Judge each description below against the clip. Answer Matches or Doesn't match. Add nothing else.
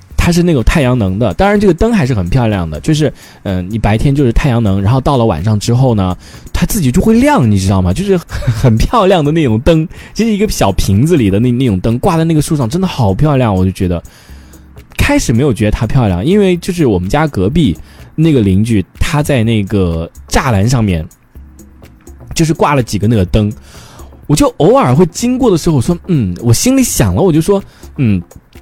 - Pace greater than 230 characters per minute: Matches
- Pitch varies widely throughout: Matches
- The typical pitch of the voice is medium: Doesn't match